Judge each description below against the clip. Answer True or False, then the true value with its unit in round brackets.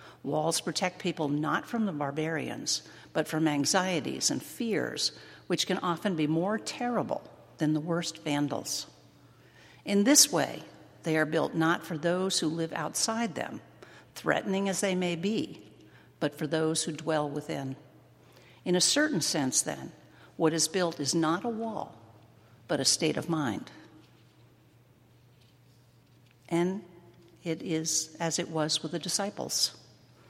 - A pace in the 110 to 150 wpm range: True (145 wpm)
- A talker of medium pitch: True (160 Hz)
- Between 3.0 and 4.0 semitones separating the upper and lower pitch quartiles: True (3.4 semitones)